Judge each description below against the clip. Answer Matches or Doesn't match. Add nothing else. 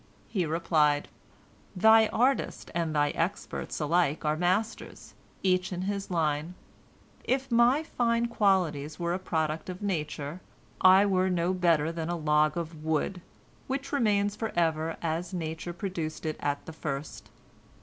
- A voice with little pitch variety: Doesn't match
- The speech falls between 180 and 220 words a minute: Doesn't match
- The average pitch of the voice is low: Doesn't match